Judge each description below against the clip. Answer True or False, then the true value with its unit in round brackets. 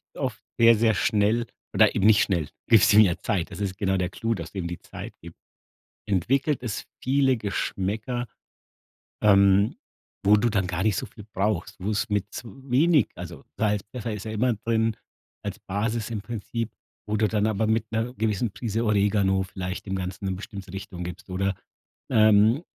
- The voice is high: False (105 Hz)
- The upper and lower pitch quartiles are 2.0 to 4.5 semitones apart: True (2.7 semitones)